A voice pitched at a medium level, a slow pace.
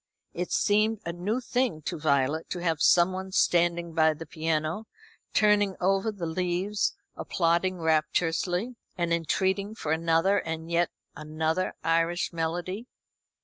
Yes: medium, 175 Hz; slow, 130 wpm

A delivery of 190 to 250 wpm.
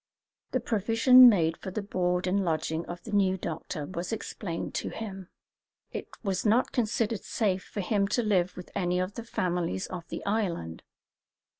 No: average, 170 wpm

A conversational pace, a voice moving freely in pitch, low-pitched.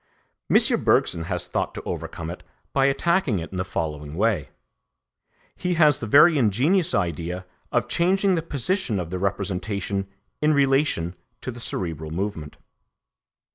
Yes: average, 145 wpm; wide, 8.7 semitones; low, 100 Hz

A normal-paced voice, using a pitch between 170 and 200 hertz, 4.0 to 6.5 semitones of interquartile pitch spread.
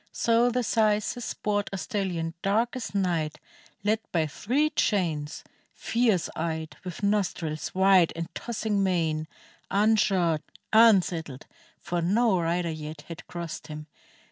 No: slow, 125 wpm; medium, 185 Hz; average, 4.5 semitones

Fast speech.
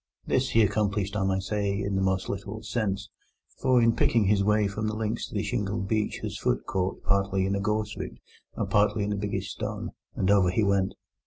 Yes: fast, 220 wpm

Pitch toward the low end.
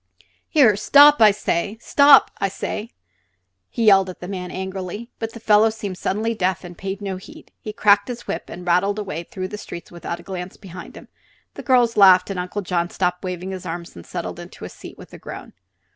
No: high, 195 Hz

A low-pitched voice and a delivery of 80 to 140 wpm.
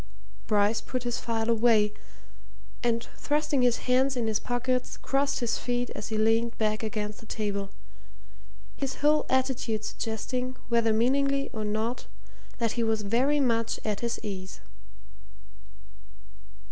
No: high, 230 Hz; slow, 135 wpm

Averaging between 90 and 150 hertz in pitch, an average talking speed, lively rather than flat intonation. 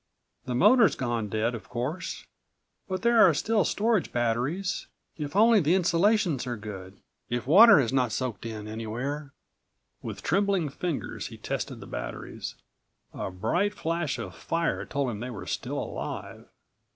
Yes: medium, 140 Hz; average, 150 wpm; wide, 8.3 semitones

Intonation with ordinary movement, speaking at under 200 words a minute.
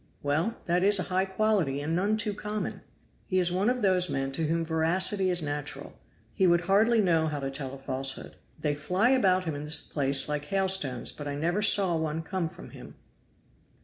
No: average, 4.7 semitones; fast, 205 wpm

